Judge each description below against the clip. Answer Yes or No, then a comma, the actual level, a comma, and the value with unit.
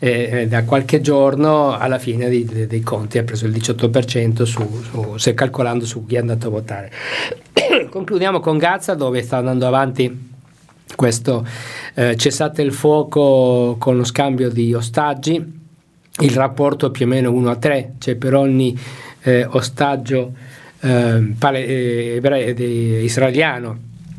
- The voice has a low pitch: Yes, low, 130 Hz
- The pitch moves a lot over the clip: No, average, 3.1 semitones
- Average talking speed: Yes, average, 145 wpm